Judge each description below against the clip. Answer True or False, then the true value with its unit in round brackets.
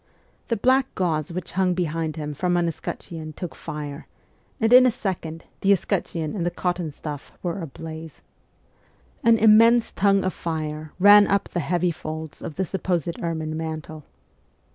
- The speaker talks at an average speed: True (160 wpm)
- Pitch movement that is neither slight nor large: True (3.6 semitones)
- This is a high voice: False (170 Hz)